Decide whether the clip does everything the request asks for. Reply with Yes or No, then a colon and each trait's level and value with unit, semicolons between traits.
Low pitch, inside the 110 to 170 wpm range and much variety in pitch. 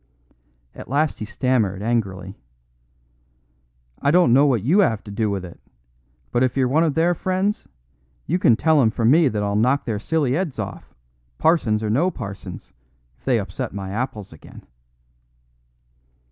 Yes: low, 120 Hz; average, 165 wpm; wide, 6.8 semitones